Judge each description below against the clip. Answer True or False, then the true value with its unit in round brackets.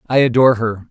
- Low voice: True (120 Hz)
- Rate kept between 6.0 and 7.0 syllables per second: True (6.5 syllables/s)